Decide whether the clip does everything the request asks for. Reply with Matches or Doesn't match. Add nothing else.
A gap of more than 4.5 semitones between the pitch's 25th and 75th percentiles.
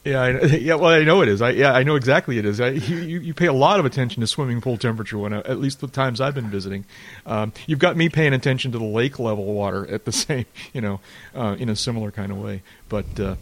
Matches